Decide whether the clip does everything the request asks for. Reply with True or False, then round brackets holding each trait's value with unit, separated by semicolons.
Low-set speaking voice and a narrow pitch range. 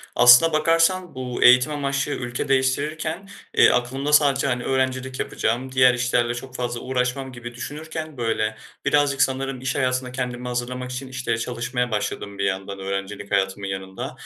True (125 Hz; 2.2 semitones)